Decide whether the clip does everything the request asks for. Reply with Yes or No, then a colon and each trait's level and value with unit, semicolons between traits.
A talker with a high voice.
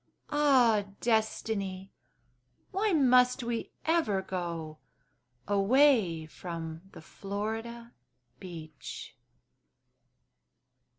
Yes: high, 210 Hz